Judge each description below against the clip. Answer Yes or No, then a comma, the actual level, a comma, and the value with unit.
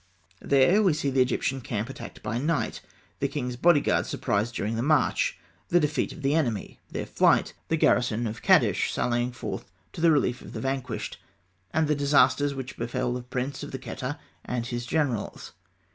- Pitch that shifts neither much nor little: Yes, average, 3.2 semitones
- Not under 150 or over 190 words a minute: Yes, average, 180 wpm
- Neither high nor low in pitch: No, low, 130 Hz